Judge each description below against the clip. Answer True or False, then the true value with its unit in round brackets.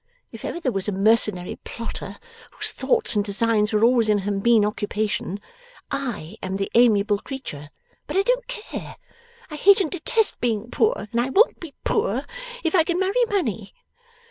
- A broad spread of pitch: True (8.8 semitones)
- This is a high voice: True (230 Hz)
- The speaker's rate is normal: True (175 wpm)